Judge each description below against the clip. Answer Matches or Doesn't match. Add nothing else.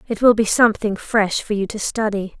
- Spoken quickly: Matches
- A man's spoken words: Doesn't match